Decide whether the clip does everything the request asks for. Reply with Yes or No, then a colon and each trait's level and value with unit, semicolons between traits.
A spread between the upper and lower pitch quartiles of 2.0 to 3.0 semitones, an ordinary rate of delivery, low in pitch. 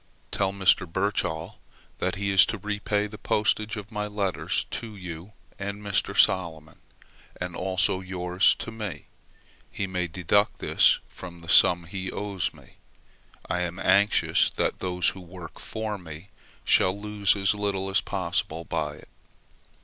Yes: narrow, 2.4 semitones; average, 150 wpm; very low, 95 Hz